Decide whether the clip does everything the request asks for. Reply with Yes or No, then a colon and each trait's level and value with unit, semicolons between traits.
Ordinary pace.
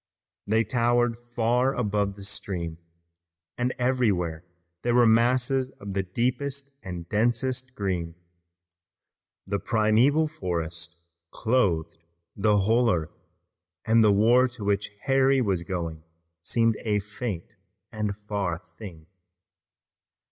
No: slow, 110 wpm